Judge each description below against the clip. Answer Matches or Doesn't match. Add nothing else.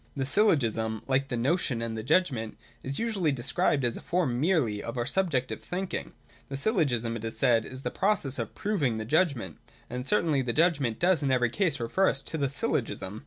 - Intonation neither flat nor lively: Doesn't match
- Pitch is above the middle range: Doesn't match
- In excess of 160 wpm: Matches